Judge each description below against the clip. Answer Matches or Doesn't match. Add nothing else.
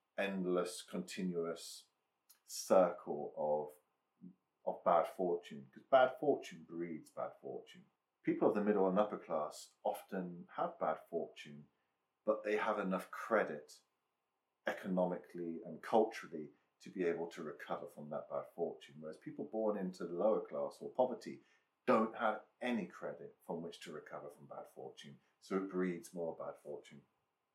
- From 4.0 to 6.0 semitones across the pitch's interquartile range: Doesn't match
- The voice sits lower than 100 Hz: Matches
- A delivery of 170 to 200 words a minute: Doesn't match